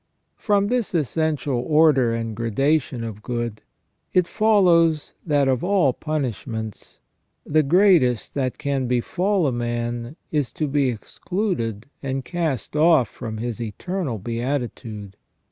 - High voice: No, low, 135 Hz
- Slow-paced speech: Yes, slow, 125 wpm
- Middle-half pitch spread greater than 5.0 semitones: Yes, wide, 5.6 semitones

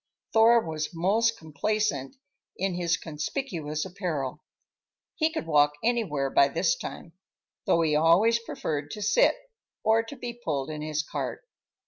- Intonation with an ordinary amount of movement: No, wide, 6.6 semitones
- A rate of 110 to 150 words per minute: Yes, slow, 135 wpm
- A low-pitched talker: No, medium, 170 Hz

